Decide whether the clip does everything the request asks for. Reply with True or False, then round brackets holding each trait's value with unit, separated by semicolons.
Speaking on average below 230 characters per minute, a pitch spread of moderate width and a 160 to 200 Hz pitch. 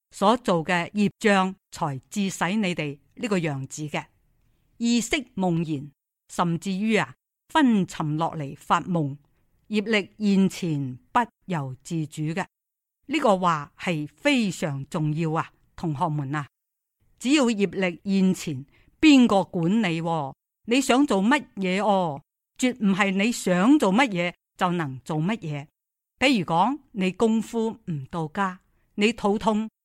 True (190 characters per minute; 5.0 semitones; 185 Hz)